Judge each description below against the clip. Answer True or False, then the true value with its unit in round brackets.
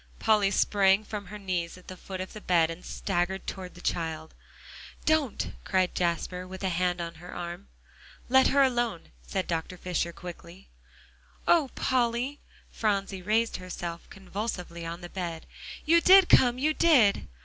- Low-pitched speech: False (190 Hz)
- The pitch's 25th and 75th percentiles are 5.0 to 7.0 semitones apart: False (4.4 semitones)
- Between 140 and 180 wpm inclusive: True (160 wpm)